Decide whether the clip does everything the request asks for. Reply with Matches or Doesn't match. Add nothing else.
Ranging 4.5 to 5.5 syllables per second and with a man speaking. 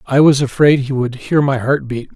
Matches